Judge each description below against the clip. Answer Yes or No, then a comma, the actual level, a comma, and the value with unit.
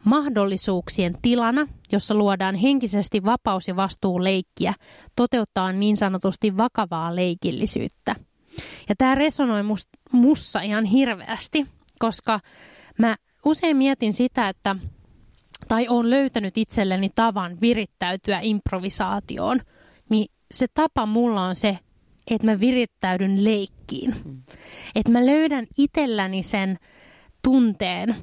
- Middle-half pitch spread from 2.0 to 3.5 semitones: No, average, 4.1 semitones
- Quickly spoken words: No, average, 100 wpm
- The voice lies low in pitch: No, high, 220 Hz